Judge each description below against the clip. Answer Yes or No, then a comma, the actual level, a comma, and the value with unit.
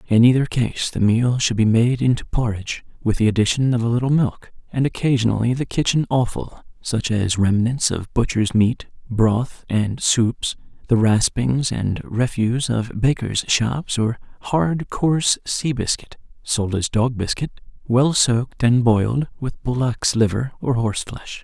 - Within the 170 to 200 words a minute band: No, average, 155 wpm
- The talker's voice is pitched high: No, low, 120 Hz